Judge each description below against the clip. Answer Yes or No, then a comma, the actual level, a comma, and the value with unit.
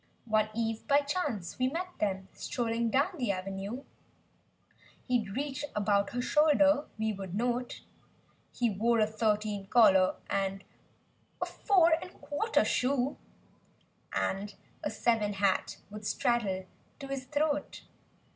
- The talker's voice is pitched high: Yes, high, 230 Hz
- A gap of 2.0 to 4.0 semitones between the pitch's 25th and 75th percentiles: No, wide, 5.6 semitones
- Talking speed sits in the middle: No, slow, 130 wpm